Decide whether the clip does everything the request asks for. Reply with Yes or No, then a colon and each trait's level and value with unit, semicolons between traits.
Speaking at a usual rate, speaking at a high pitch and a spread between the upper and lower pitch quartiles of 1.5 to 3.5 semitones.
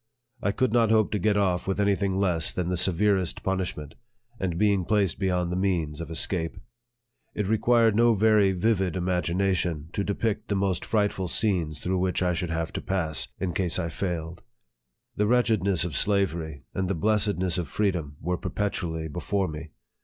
No: average, 180 wpm; very low, 95 Hz; average, 3.1 semitones